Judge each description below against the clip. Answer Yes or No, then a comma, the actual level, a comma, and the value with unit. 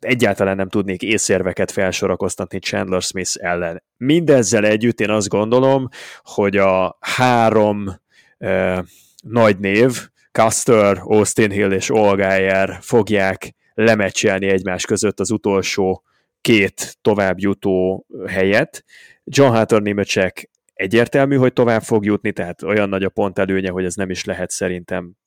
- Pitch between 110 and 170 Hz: No, low, 100 Hz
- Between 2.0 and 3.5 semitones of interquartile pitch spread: Yes, average, 2.7 semitones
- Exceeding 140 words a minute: No, average, 125 wpm